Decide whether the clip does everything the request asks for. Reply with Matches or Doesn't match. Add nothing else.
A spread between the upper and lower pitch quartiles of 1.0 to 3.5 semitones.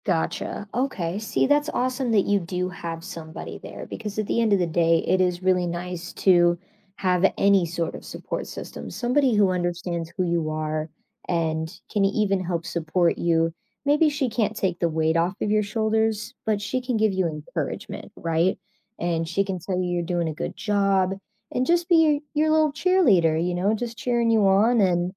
Doesn't match